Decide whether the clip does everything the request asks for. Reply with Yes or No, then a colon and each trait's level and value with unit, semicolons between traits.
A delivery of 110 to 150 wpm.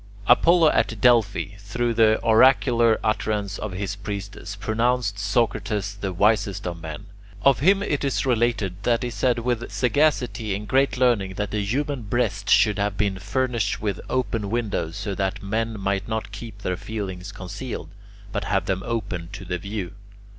No: average, 165 wpm